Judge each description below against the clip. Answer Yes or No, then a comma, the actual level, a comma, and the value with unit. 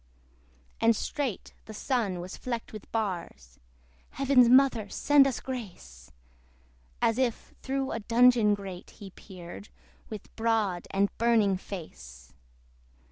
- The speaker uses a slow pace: Yes, slow, 120 wpm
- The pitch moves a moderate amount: Yes, average, 4.7 semitones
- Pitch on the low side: No, high, 215 Hz